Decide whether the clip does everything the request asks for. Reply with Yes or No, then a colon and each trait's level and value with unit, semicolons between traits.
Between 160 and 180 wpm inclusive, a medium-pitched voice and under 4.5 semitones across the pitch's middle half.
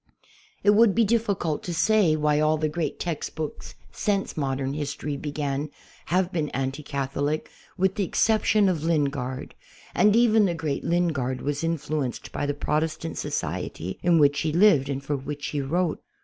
Yes: average, 170 wpm; medium, 155 Hz; average, 3.9 semitones